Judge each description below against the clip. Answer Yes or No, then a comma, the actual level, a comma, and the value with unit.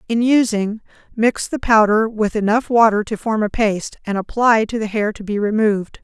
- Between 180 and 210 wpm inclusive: Yes, average, 200 wpm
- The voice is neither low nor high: No, high, 215 Hz